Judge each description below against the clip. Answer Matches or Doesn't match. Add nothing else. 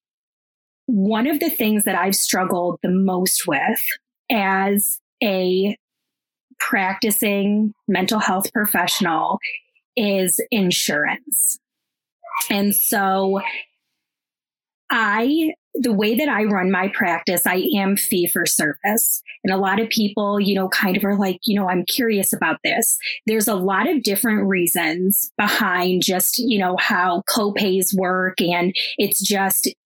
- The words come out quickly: Doesn't match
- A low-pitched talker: Doesn't match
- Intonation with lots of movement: Doesn't match